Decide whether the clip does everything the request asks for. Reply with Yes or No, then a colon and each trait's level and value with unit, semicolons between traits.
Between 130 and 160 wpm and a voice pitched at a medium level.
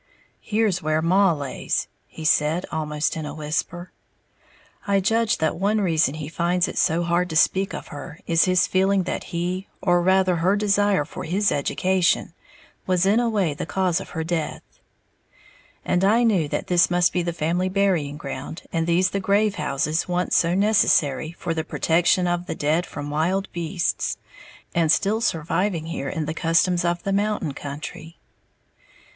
No: average, 175 wpm; medium, 175 Hz